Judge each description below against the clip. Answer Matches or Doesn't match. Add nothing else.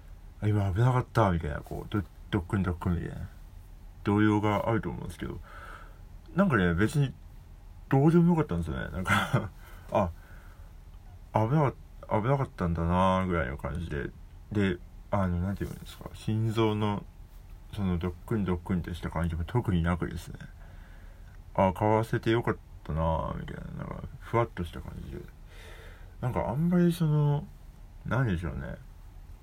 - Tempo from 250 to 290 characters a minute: Doesn't match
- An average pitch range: Matches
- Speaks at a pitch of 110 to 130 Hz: Doesn't match